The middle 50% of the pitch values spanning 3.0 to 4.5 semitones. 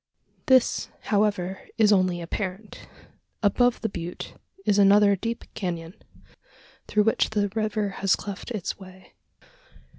No: narrow, 2.4 semitones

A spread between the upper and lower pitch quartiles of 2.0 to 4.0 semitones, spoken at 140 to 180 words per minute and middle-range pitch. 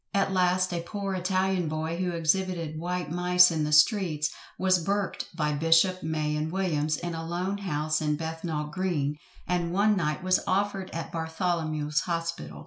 Yes: average, 3.0 semitones; average, 165 wpm; medium, 170 Hz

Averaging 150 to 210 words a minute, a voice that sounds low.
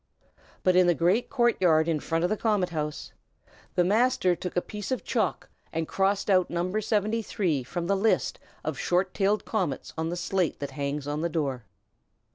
No: average, 190 wpm; medium, 180 Hz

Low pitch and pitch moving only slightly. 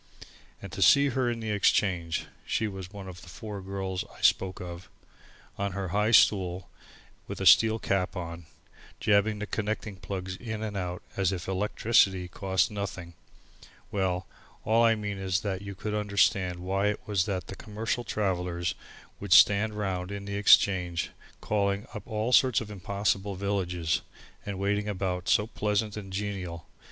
Yes: low, 100 Hz; narrow, 2.3 semitones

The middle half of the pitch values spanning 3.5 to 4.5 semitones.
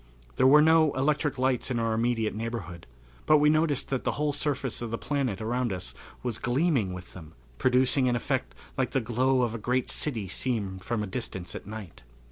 Yes: average, 3.9 semitones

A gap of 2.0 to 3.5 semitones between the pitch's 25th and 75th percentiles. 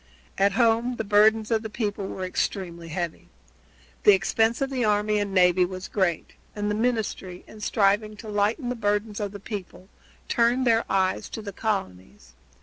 Yes: average, 2.8 semitones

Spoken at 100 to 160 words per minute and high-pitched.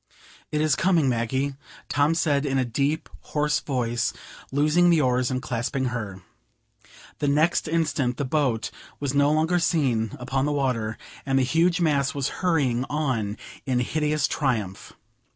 No: average, 150 wpm; medium, 140 Hz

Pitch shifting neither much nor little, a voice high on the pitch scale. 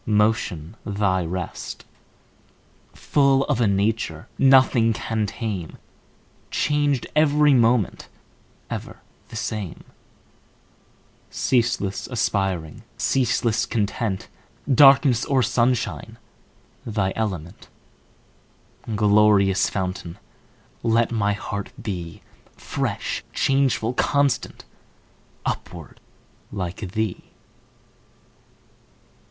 No: average, 4.3 semitones; low, 110 Hz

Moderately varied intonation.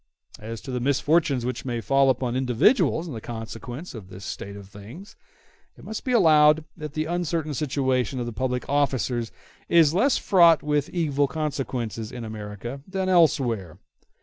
Yes: average, 4.9 semitones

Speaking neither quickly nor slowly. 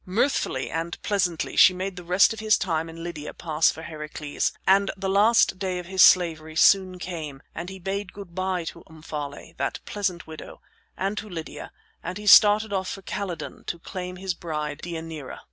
Yes: average, 185 wpm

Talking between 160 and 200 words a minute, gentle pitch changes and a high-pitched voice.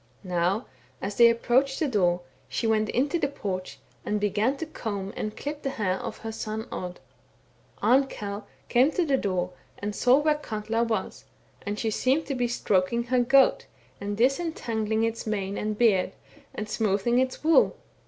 No: average, 175 wpm; average, 4.1 semitones; high, 225 Hz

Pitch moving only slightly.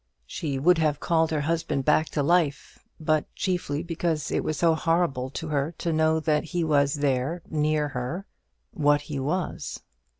Yes: narrow, 2.3 semitones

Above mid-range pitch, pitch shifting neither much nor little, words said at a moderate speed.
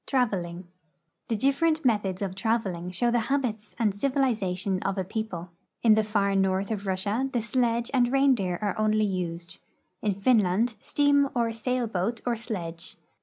Yes: high, 215 Hz; average, 4.1 semitones; average, 170 wpm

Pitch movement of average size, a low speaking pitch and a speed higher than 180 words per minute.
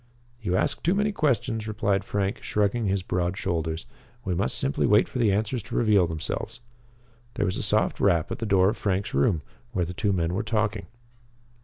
Yes: average, 3.2 semitones; low, 100 Hz; average, 195 wpm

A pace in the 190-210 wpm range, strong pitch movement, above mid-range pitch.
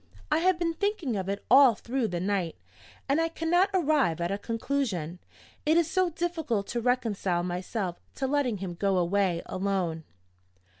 No: average, 165 wpm; wide, 9.0 semitones; high, 230 Hz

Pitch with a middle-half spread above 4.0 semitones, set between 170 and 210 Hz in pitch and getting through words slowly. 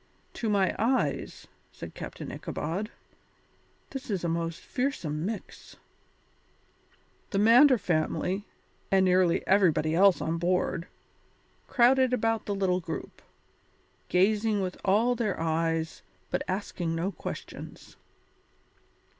Yes: average, 4.6 semitones; high, 190 Hz; slow, 110 wpm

